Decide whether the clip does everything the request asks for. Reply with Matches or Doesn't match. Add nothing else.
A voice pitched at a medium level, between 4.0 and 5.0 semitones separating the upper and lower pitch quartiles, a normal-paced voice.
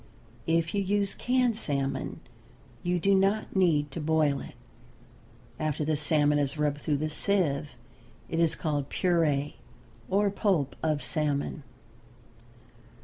Doesn't match